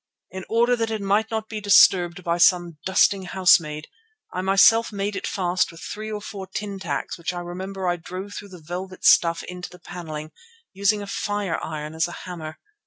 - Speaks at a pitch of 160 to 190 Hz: Yes, medium, 185 Hz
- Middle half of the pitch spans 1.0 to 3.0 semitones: Yes, average, 2.7 semitones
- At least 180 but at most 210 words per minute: Yes, average, 190 wpm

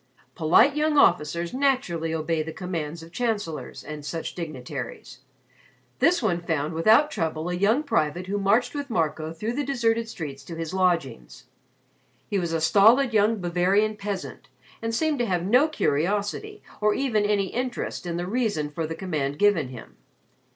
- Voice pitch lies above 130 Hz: Yes, medium, 185 Hz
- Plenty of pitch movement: Yes, wide, 5.9 semitones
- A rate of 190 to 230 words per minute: No, average, 165 wpm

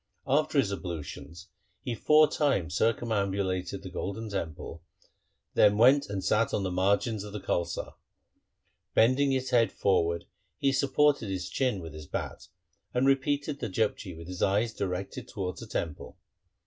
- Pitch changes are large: Yes, wide, 5.9 semitones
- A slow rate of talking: No, average, 155 wpm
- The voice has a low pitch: Yes, low, 105 Hz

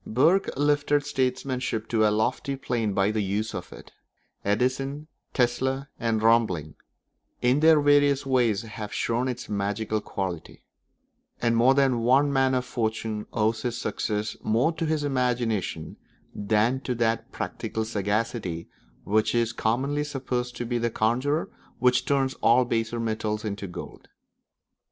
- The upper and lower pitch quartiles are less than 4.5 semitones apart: Yes, average, 3.5 semitones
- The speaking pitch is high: No, low, 120 Hz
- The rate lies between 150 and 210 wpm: No, average, 140 wpm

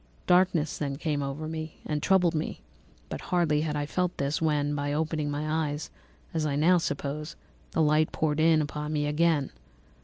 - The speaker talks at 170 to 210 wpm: Yes, average, 180 wpm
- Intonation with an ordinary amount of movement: No, narrow, 1.6 semitones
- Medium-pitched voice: Yes, medium, 155 Hz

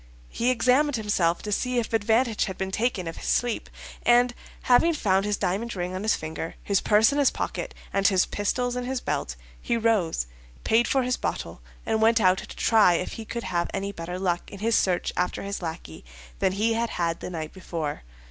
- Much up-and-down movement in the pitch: No, average, 4.5 semitones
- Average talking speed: No, fast, 210 wpm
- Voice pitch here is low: No, high, 210 Hz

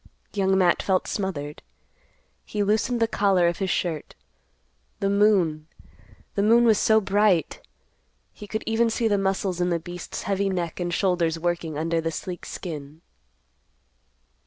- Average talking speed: Yes, average, 145 wpm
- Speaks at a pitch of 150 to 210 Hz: Yes, high, 190 Hz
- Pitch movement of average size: Yes, average, 3.3 semitones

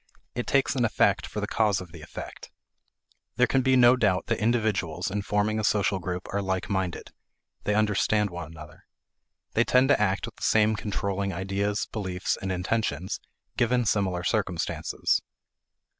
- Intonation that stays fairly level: No, average, 3.0 semitones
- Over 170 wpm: No, average, 165 wpm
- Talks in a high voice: No, low, 100 Hz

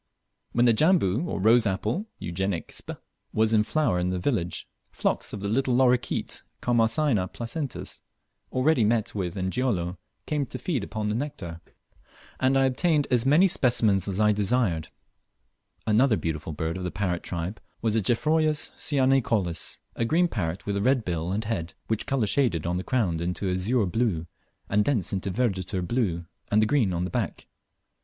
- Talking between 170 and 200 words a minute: Yes, average, 175 wpm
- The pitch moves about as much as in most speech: No, wide, 5.7 semitones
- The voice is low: Yes, low, 110 Hz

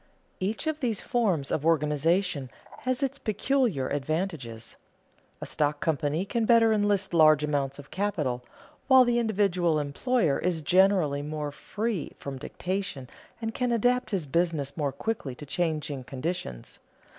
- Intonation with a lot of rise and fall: Yes, wide, 6.8 semitones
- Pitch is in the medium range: Yes, medium, 170 Hz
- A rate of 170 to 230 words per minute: No, average, 140 wpm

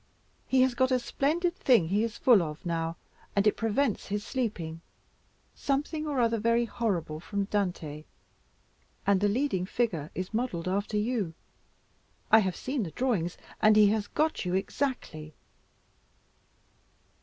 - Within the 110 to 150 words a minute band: Yes, average, 145 wpm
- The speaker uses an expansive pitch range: Yes, wide, 5.7 semitones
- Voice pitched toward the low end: No, high, 210 Hz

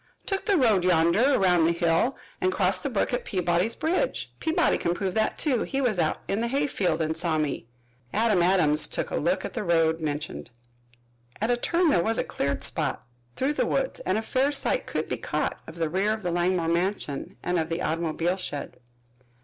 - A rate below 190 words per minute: No, fast, 205 wpm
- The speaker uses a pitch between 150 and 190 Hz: Yes, medium, 185 Hz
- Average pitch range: No, wide, 6.0 semitones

